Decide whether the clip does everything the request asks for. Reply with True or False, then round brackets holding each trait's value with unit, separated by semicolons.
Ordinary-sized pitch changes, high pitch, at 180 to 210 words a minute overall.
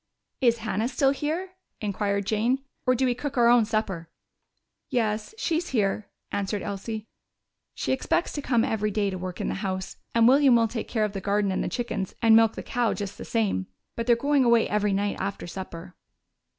True (3.4 semitones; 220 Hz; 200 wpm)